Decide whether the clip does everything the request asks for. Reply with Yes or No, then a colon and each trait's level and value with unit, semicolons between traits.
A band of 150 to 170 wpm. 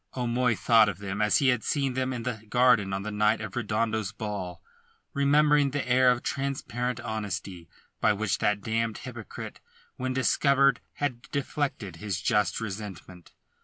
Yes: average, 160 wpm